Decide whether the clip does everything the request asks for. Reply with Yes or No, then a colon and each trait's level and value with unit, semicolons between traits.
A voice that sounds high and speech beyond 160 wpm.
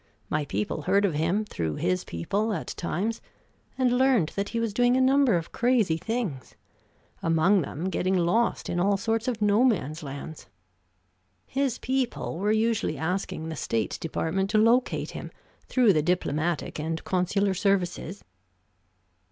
No: high, 195 Hz; average, 150 wpm